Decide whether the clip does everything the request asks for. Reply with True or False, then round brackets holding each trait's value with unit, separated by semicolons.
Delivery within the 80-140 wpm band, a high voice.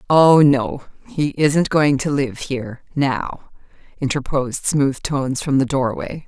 False (135 wpm; 140 Hz)